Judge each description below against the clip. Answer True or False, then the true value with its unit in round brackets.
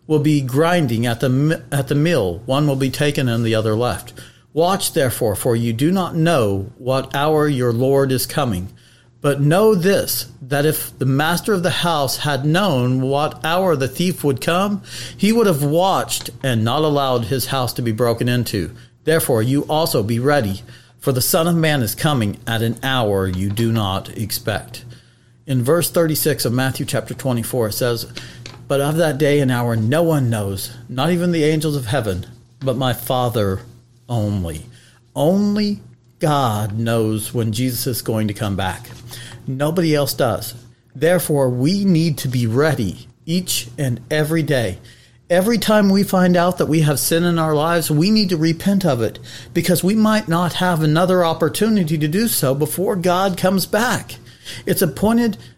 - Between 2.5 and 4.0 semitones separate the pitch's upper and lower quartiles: False (5.3 semitones)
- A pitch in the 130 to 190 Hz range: True (135 Hz)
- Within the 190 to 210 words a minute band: False (175 wpm)